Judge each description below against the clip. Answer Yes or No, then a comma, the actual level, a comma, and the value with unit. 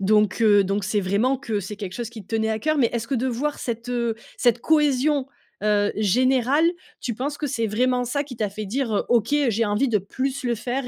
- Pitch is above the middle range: Yes, high, 235 Hz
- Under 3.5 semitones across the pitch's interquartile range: No, average, 3.9 semitones